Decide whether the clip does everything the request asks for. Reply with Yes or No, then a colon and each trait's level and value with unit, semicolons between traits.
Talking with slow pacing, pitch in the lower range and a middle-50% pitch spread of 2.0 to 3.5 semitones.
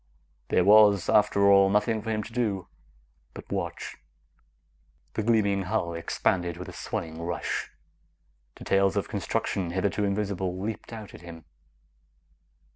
Yes: slow, 130 wpm; low, 100 Hz; average, 2.9 semitones